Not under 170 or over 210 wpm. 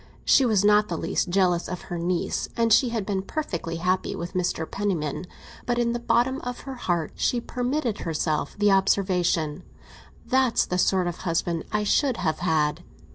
Yes: average, 180 wpm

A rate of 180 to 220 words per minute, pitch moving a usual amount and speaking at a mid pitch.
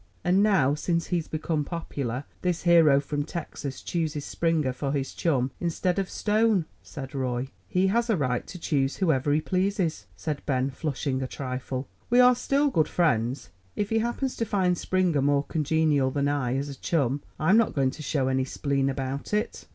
Yes: average, 185 wpm; average, 5.0 semitones; medium, 150 Hz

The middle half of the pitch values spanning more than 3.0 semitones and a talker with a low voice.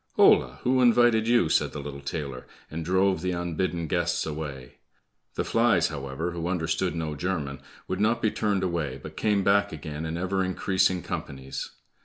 Yes: average, 4.3 semitones; very low, 85 Hz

